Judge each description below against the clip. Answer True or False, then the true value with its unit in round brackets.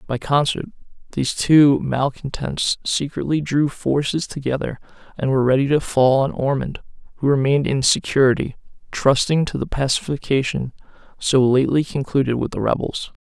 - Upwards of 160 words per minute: False (135 wpm)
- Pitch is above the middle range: False (135 Hz)